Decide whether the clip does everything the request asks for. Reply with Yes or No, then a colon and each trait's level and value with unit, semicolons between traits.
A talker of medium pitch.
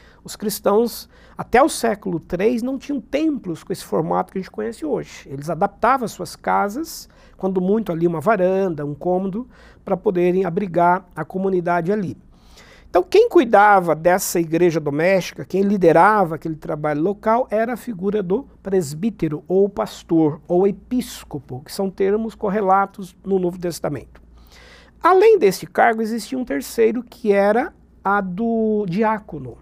No: high, 195 Hz